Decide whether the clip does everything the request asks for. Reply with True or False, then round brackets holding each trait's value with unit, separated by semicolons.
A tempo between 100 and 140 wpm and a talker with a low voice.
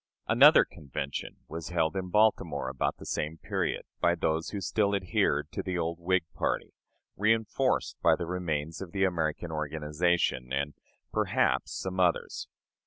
False (150 wpm; 85 Hz)